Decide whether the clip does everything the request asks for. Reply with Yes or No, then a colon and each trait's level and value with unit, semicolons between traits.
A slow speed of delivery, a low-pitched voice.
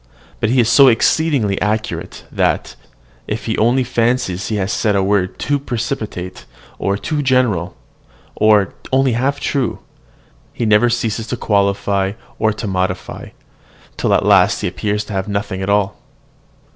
No: average, 160 wpm; low, 110 Hz